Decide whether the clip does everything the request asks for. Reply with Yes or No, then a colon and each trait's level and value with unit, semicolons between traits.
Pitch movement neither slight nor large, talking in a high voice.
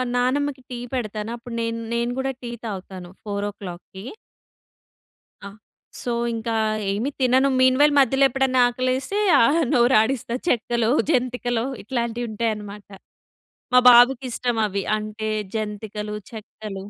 Yes: average, 3.2 semitones; high, 235 Hz